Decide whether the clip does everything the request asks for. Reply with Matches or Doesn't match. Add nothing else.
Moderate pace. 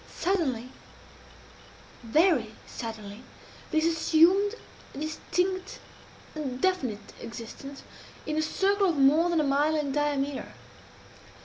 Doesn't match